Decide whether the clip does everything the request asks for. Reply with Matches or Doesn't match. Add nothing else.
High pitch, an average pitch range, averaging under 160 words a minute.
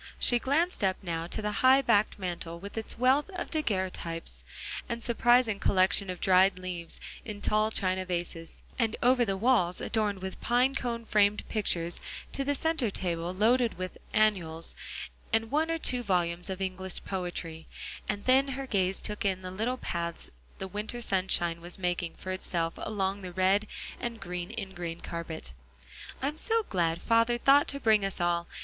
Doesn't match